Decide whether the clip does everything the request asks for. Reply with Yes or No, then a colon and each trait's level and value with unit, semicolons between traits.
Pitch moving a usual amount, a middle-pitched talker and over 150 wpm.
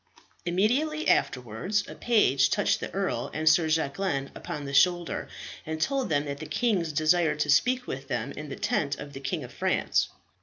No: wide, 5.8 semitones; medium, 155 Hz; average, 185 wpm